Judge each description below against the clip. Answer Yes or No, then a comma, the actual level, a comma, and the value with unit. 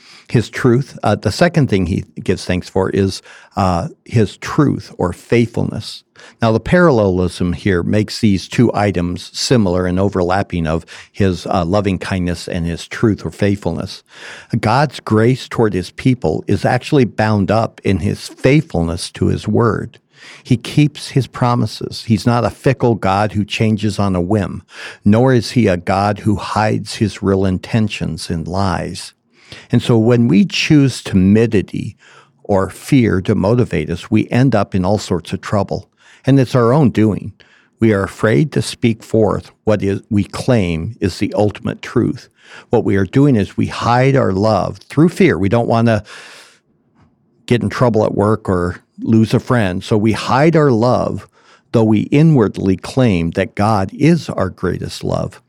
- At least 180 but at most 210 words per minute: No, average, 170 wpm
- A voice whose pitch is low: Yes, low, 105 Hz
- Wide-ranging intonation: No, average, 4.0 semitones